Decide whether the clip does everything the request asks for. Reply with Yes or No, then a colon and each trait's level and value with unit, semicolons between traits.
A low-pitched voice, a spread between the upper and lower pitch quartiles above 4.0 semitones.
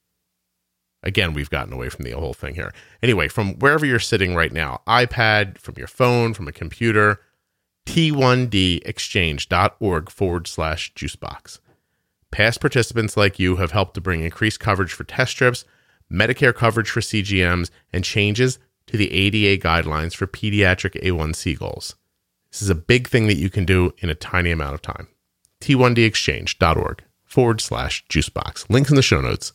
Yes: low, 100 Hz; average, 4.7 semitones